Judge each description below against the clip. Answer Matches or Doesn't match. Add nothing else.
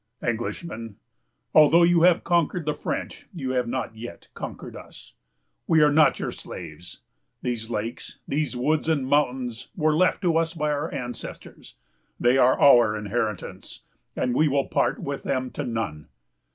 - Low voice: Matches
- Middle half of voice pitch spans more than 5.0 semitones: Doesn't match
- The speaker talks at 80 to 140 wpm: Doesn't match